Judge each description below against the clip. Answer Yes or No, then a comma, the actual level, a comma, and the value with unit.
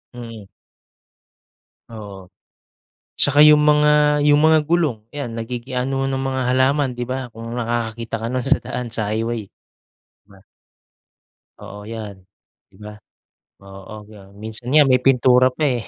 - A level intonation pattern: No, average, 3.5 semitones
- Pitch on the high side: No, low, 125 Hz